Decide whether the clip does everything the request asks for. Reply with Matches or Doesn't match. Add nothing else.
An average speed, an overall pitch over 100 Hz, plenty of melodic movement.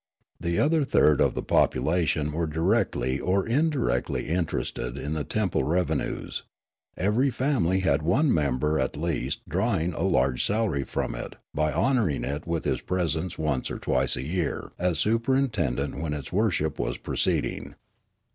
Doesn't match